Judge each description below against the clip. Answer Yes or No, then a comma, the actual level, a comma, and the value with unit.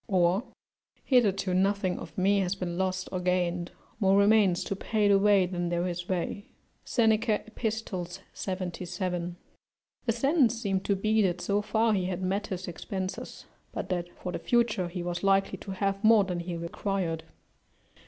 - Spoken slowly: No, average, 165 wpm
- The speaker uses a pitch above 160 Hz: Yes, high, 190 Hz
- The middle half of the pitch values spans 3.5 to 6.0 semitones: No, narrow, 2.4 semitones